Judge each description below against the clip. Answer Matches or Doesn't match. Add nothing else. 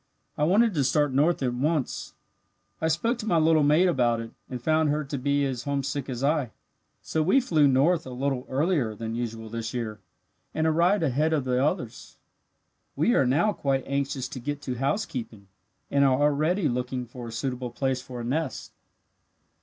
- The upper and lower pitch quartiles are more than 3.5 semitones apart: Matches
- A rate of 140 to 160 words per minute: Doesn't match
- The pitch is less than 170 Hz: Matches